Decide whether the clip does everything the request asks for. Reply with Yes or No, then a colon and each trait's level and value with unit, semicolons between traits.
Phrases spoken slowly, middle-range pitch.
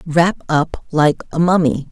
No: average, 155 wpm; medium, 160 Hz